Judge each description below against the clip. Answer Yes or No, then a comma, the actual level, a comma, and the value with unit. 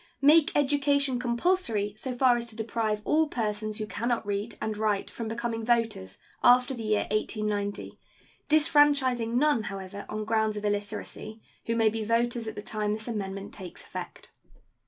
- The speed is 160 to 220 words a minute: Yes, average, 165 wpm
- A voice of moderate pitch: No, high, 225 Hz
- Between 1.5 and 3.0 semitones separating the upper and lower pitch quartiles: Yes, average, 2.7 semitones